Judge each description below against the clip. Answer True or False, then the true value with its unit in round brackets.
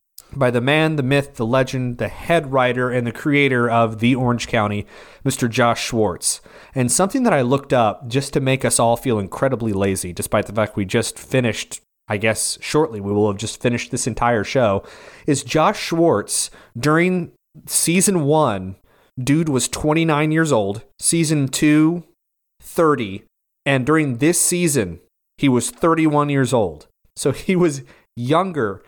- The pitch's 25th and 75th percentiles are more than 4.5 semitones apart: True (5.0 semitones)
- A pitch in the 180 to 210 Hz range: False (130 Hz)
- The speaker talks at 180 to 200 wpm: False (160 wpm)